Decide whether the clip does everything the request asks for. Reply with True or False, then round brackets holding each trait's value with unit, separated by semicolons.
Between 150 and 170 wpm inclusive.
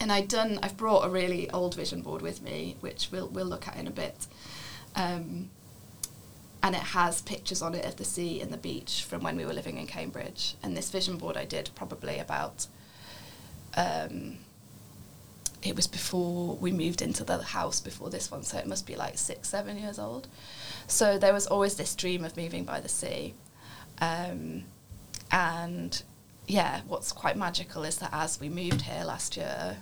False (190 wpm)